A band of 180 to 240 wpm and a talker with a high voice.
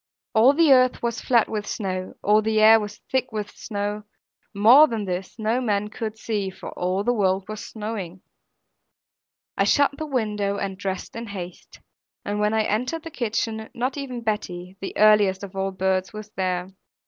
Yes: average, 185 wpm; high, 210 Hz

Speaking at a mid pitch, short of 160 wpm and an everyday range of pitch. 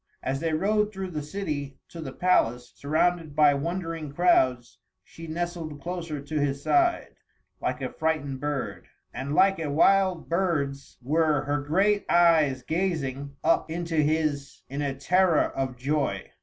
Yes: medium, 155 Hz; average, 150 wpm; average, 3.7 semitones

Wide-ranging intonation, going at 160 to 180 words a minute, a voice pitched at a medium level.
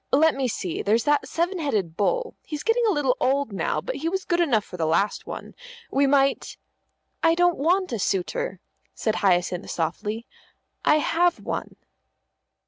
No: wide, 8.6 semitones; average, 175 wpm; very high, 280 Hz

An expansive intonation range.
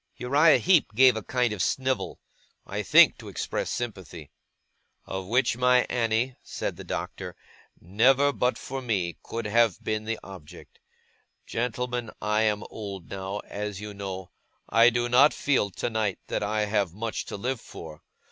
No: average, 3.7 semitones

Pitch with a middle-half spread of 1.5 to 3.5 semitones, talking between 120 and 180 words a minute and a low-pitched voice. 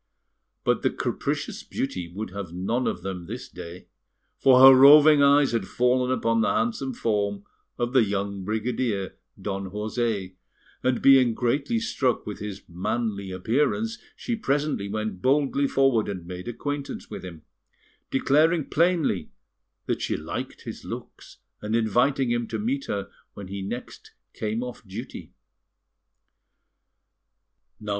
No: average, 5.2 semitones; slow, 135 wpm; low, 115 Hz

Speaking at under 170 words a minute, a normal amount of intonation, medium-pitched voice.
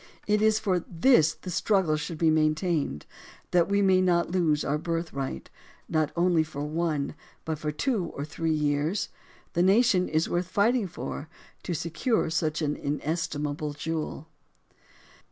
Yes: average, 155 wpm; average, 3.2 semitones; medium, 165 Hz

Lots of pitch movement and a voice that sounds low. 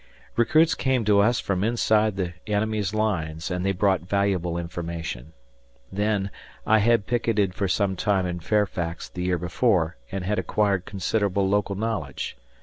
No: average, 3.0 semitones; low, 100 Hz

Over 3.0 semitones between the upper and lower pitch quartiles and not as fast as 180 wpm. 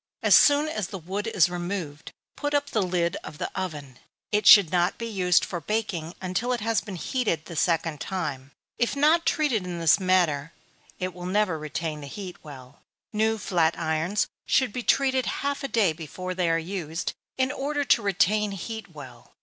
No: average, 5.1 semitones; average, 190 wpm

